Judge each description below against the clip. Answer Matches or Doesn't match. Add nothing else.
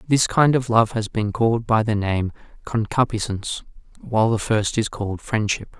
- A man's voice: Matches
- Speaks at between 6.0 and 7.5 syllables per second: Doesn't match